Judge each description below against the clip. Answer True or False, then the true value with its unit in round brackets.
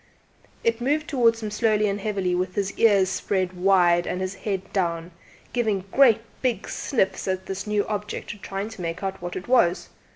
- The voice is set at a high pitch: True (195 Hz)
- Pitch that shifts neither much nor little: True (3.0 semitones)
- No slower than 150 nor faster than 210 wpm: True (185 wpm)